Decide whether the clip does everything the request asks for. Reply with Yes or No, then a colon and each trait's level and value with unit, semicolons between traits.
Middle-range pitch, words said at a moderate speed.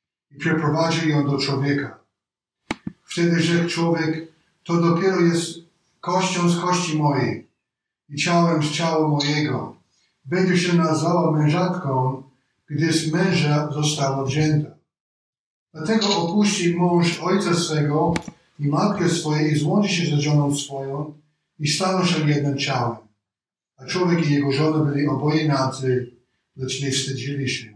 Yes: medium, 155 Hz; average, 130 wpm